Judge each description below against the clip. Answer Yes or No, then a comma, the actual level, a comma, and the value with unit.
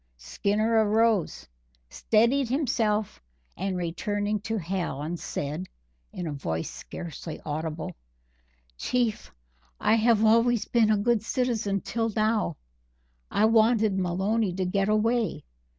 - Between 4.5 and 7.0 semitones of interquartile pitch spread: No, average, 4.0 semitones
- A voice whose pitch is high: Yes, high, 210 Hz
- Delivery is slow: Yes, slow, 115 wpm